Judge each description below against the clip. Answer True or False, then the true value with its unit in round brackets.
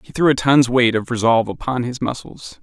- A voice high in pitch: False (125 Hz)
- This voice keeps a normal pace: False (230 wpm)